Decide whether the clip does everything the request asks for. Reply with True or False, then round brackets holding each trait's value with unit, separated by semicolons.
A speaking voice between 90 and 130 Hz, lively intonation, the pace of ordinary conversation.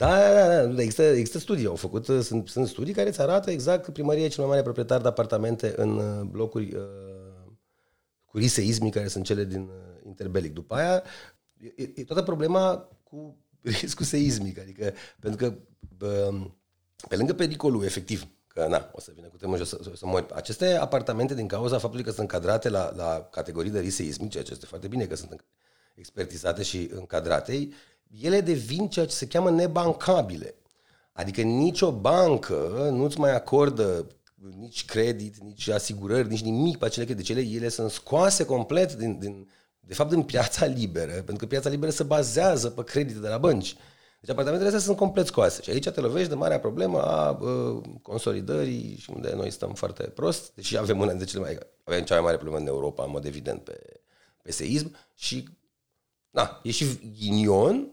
False (115 Hz; 6.8 semitones; 180 wpm)